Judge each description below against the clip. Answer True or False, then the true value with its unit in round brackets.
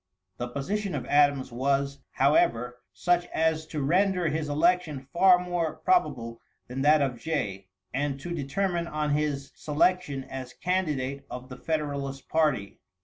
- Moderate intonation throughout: True (4.0 semitones)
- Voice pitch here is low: False (145 Hz)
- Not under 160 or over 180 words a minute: False (145 wpm)